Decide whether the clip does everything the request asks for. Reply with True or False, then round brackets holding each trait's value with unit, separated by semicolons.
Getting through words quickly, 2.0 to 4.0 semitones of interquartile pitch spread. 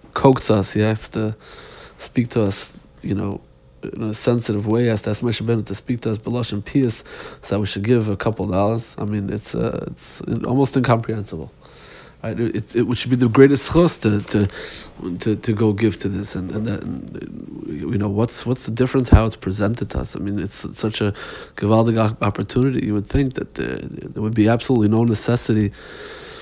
True (205 wpm; 2.9 semitones)